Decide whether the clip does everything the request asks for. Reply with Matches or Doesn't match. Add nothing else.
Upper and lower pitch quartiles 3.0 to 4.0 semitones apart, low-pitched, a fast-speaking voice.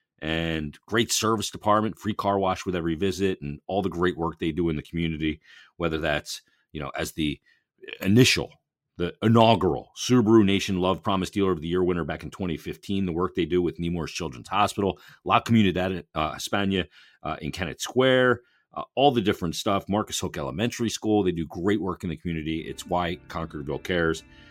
Doesn't match